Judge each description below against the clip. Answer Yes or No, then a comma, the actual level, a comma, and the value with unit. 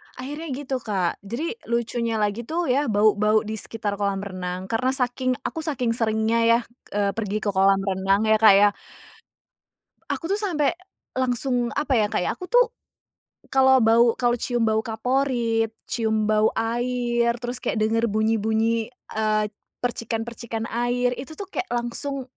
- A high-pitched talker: Yes, high, 230 Hz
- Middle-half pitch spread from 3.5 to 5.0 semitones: No, average, 2.7 semitones